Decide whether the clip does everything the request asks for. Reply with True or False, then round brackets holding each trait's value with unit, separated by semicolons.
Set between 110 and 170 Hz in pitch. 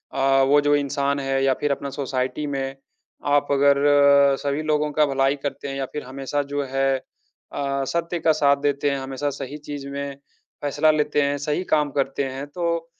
True (140 Hz)